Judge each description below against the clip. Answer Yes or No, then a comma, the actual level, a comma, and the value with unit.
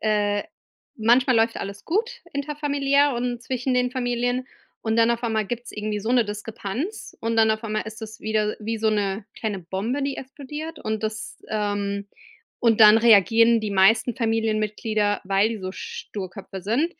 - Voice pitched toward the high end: Yes, high, 225 Hz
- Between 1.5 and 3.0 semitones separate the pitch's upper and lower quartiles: Yes, average, 2.7 semitones